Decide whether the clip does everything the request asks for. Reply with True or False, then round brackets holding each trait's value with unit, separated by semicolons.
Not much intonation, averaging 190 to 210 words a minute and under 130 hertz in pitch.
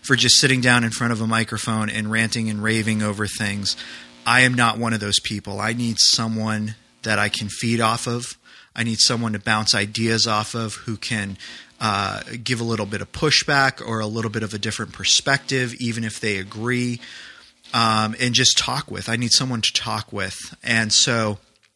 True (1.7 semitones; 200 wpm; 110 Hz)